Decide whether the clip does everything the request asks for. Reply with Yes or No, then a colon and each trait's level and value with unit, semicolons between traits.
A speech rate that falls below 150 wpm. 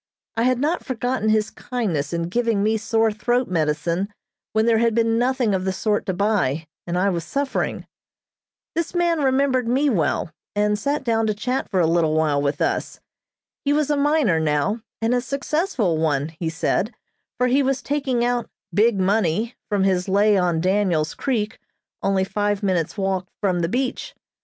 No: average, 180 wpm